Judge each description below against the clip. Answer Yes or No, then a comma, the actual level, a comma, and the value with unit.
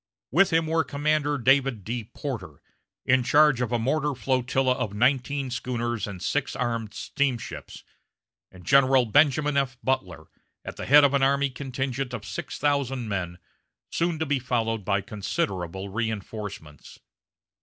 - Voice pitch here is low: Yes, low, 125 Hz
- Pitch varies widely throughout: No, average, 4.3 semitones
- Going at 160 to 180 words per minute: No, average, 145 wpm